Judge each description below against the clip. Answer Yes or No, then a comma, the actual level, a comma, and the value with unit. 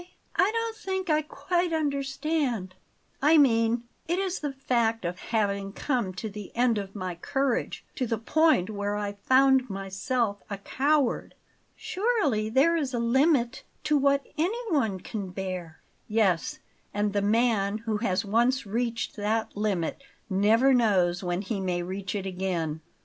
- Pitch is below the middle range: No, high, 225 Hz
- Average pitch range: No, wide, 5.8 semitones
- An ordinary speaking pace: Yes, average, 150 wpm